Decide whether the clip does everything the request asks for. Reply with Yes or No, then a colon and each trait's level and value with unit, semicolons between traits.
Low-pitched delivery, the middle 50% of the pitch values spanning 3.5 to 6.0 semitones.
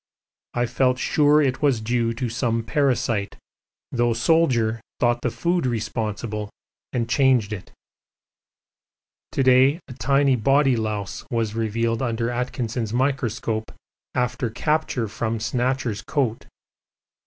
No: low, 120 Hz; average, 2.8 semitones